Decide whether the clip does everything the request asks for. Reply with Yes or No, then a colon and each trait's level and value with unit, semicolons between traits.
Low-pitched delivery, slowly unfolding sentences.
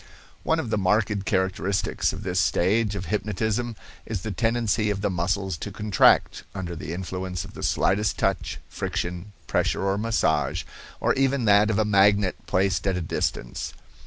No: low, 100 Hz; average, 165 wpm